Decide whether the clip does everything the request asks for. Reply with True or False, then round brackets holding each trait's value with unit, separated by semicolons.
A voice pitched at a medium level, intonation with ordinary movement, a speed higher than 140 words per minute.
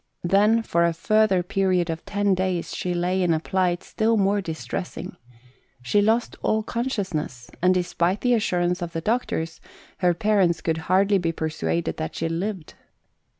True (180 Hz; 3.3 semitones; 160 wpm)